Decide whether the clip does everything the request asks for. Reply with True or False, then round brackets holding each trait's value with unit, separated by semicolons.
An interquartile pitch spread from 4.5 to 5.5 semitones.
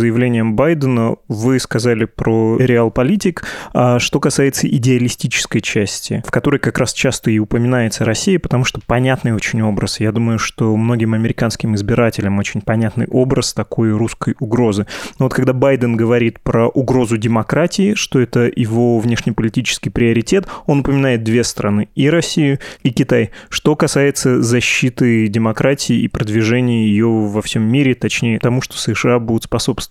False (2.8 semitones)